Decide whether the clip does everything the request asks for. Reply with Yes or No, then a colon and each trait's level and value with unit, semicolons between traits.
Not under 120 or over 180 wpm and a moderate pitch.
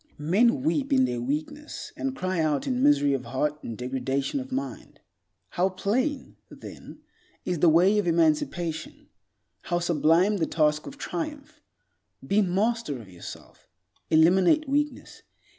Yes: average, 140 wpm; medium, 180 Hz